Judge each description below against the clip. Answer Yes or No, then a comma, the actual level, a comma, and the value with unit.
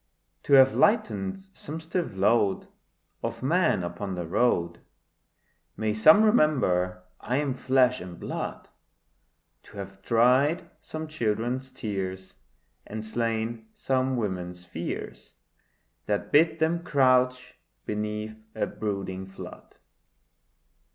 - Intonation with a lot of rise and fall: Yes, wide, 6.1 semitones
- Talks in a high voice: No, low, 115 Hz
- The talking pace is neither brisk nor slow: No, slow, 110 wpm